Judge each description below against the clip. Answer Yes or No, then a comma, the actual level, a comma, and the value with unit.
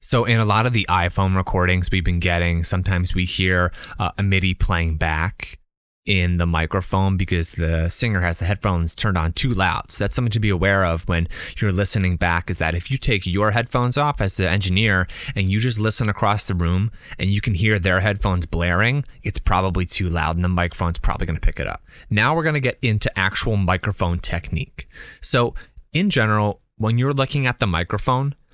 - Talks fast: Yes, fast, 210 wpm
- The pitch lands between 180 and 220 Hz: No, very low, 95 Hz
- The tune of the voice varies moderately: Yes, average, 3.8 semitones